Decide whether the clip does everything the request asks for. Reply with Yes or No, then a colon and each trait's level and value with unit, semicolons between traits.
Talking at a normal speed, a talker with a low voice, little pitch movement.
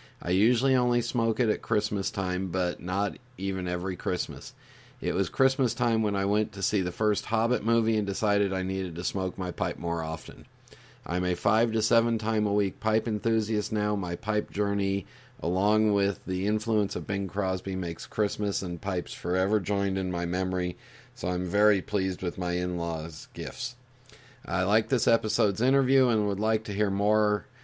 No: average, 185 wpm; low, 100 Hz; average, 3.1 semitones